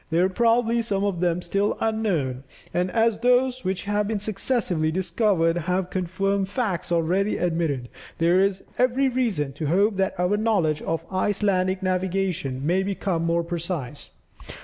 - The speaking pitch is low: No, medium, 185 Hz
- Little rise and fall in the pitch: No, average, 3.5 semitones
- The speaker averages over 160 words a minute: No, average, 150 wpm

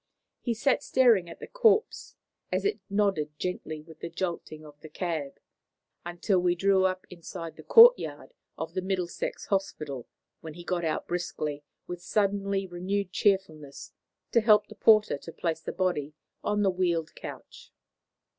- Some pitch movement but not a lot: Yes, average, 3.6 semitones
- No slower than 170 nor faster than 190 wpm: No, average, 155 wpm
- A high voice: No, medium, 180 Hz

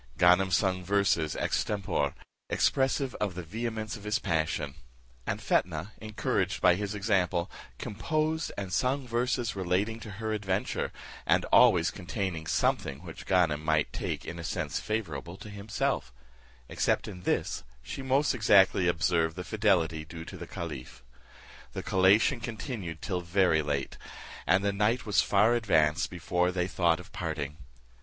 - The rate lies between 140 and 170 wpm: Yes, average, 150 wpm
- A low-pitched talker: Yes, very low, 95 Hz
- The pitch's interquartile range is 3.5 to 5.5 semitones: Yes, average, 4.2 semitones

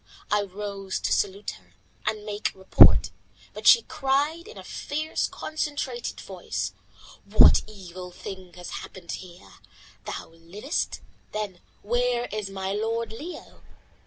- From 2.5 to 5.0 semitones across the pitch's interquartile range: Yes, average, 4.6 semitones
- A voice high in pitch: Yes, high, 210 Hz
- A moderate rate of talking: No, slow, 130 wpm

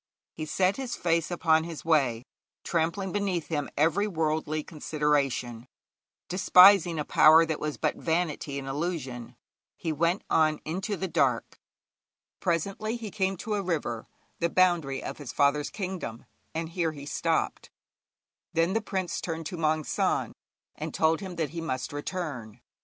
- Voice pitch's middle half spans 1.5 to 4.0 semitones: Yes, average, 3.6 semitones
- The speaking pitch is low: No, medium, 160 Hz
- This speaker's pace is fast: No, average, 150 wpm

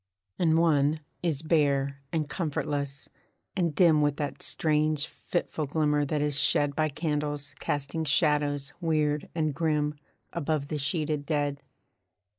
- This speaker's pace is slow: Yes, slow, 130 wpm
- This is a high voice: No, medium, 150 Hz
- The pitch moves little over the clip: Yes, narrow, 1.6 semitones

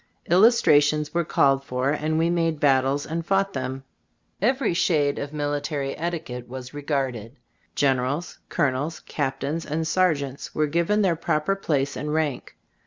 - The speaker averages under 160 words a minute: Yes, average, 145 wpm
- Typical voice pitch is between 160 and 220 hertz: No, medium, 150 Hz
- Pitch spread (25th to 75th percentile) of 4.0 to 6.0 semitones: No, average, 3.4 semitones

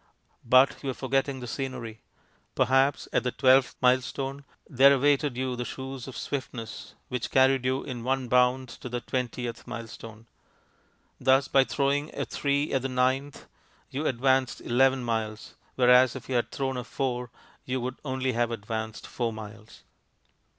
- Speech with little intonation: Yes, narrow, 1.8 semitones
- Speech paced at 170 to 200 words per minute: No, average, 155 wpm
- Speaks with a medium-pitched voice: No, low, 130 Hz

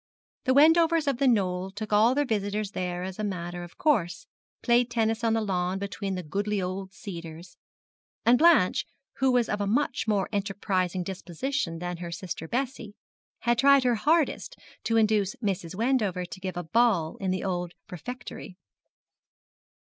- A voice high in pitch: Yes, high, 205 Hz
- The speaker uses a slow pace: No, average, 165 wpm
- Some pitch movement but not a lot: Yes, average, 4.9 semitones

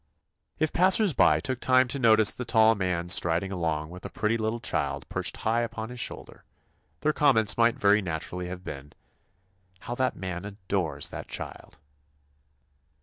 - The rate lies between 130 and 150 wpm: No, average, 160 wpm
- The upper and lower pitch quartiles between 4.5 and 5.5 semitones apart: Yes, average, 5.1 semitones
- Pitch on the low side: Yes, low, 105 Hz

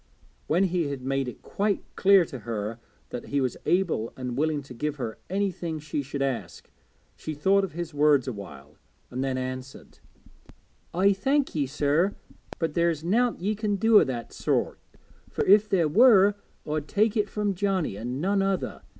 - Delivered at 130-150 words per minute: No, average, 180 wpm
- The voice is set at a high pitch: No, medium, 155 Hz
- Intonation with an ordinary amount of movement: No, wide, 6.8 semitones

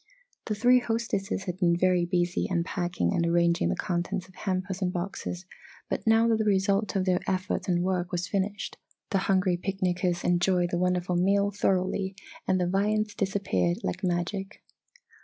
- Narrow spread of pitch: Yes, narrow, 2.1 semitones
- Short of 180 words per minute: Yes, average, 165 wpm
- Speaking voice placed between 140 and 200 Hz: Yes, medium, 185 Hz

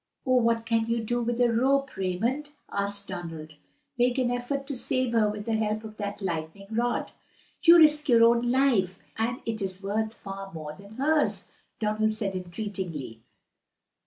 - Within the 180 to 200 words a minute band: No, average, 165 wpm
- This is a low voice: No, high, 220 Hz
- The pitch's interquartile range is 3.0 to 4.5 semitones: Yes, average, 3.7 semitones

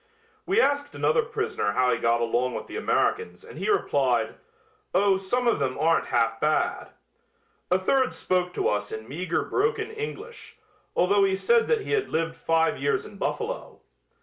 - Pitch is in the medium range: No, high, 195 Hz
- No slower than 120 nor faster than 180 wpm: Yes, average, 175 wpm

